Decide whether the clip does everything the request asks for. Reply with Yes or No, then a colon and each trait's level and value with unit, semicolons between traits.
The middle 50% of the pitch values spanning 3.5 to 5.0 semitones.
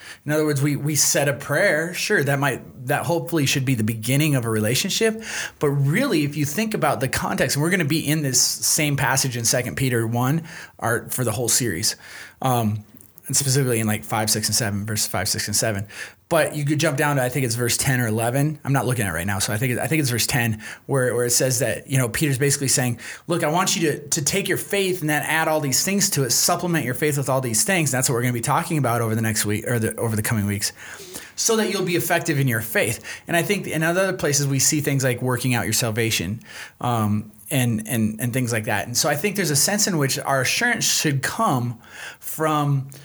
Yes: average, 4.5 semitones